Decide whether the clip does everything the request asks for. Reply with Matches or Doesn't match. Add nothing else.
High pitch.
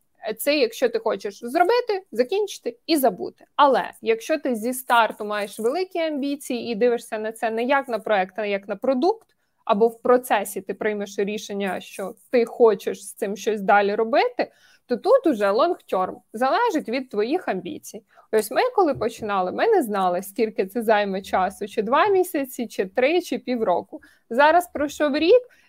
Matches